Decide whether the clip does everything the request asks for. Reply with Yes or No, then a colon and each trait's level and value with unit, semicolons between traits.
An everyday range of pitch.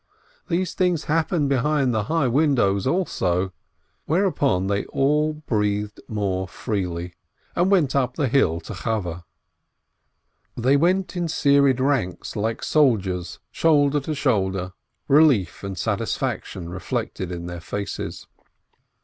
No: wide, 7.9 semitones